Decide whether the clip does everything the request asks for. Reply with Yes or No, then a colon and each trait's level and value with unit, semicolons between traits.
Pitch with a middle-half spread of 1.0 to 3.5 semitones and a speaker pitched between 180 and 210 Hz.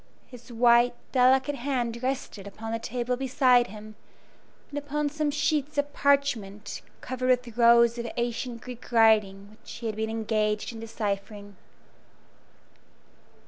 No: average, 2.8 semitones; high, 235 Hz